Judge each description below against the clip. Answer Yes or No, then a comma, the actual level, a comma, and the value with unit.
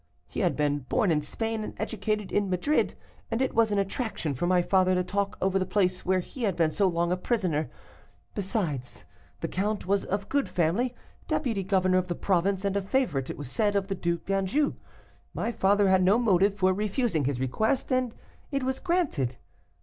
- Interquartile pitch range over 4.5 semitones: No, average, 3.5 semitones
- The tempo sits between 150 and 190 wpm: No, average, 200 wpm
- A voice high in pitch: Yes, high, 195 Hz